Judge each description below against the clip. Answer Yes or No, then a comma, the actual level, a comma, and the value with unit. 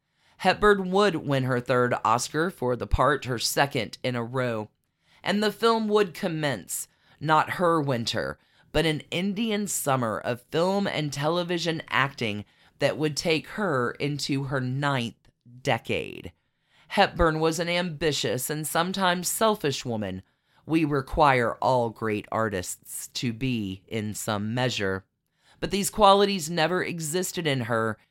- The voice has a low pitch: No, medium, 145 Hz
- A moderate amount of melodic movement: No, wide, 6.3 semitones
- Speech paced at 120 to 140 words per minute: Yes, slow, 135 wpm